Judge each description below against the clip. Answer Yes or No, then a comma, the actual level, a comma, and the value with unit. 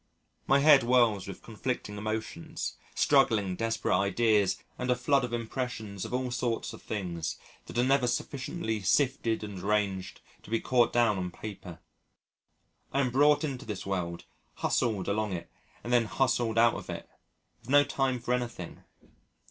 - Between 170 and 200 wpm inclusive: No, average, 160 wpm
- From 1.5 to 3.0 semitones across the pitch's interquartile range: No, average, 4.0 semitones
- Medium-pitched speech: No, low, 115 Hz